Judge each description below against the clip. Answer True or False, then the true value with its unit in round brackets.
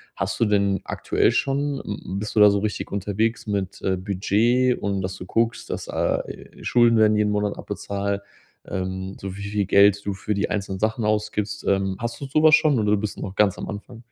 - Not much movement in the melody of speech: True (1.9 semitones)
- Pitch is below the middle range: True (105 Hz)